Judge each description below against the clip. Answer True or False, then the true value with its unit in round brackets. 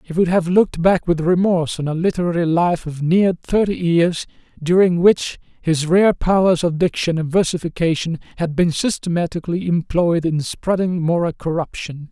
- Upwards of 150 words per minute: True (160 wpm)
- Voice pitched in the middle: True (170 Hz)